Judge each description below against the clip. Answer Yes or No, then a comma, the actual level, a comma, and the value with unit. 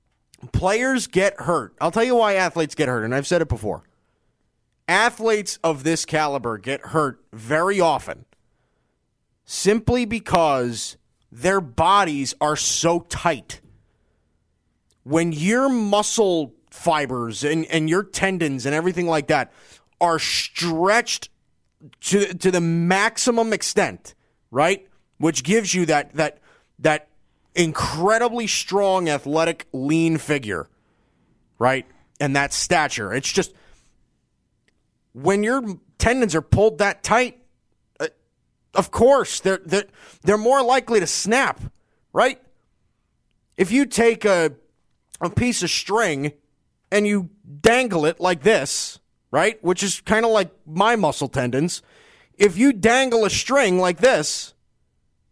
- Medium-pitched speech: Yes, medium, 180 Hz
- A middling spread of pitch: No, wide, 5.9 semitones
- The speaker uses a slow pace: Yes, slow, 125 wpm